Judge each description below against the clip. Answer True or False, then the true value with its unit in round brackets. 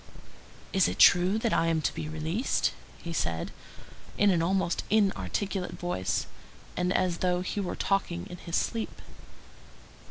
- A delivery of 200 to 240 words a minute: False (150 wpm)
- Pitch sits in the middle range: True (180 Hz)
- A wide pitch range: False (2.9 semitones)